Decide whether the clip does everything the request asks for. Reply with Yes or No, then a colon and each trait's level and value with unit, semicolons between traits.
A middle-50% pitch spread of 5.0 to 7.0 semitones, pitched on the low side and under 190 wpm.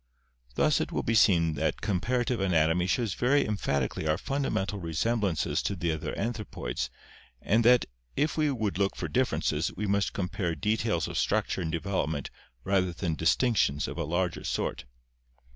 Yes: average, 5.3 semitones; very low, 95 Hz; average, 160 wpm